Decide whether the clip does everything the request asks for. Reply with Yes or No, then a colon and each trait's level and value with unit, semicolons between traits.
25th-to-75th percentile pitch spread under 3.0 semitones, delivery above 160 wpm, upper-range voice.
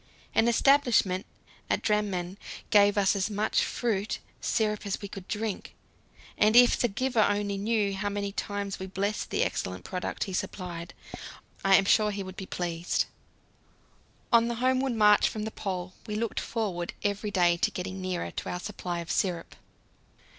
Yes: narrow, 2.5 semitones; average, 170 wpm; high, 200 Hz